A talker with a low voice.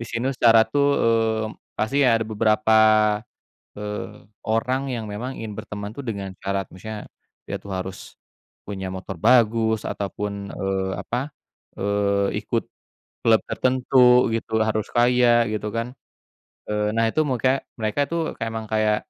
Yes: low, 110 Hz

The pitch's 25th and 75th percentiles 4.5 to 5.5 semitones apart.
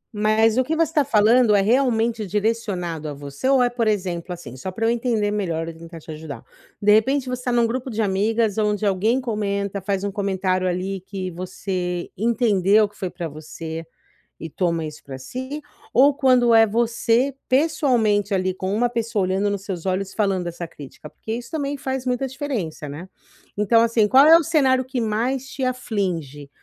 Yes: average, 4.8 semitones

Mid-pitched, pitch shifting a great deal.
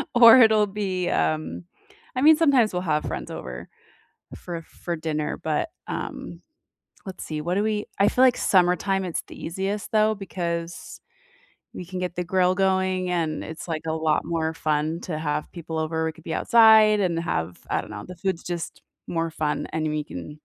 No: medium, 175 Hz; average, 3.7 semitones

